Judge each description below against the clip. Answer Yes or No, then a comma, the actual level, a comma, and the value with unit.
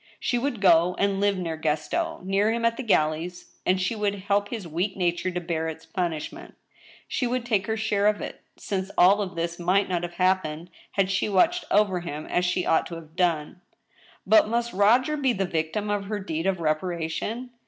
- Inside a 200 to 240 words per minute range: Yes, fast, 205 wpm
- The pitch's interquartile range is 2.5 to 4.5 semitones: Yes, average, 3.6 semitones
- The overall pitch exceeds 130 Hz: Yes, high, 190 Hz